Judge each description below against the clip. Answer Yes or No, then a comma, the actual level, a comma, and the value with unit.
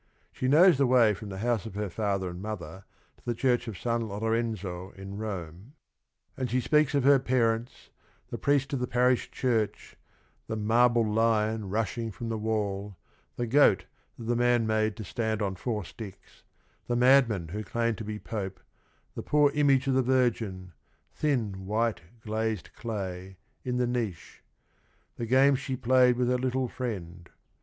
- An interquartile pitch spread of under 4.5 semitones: Yes, average, 3.4 semitones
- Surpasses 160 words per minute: Yes, average, 170 wpm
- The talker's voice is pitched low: Yes, low, 115 Hz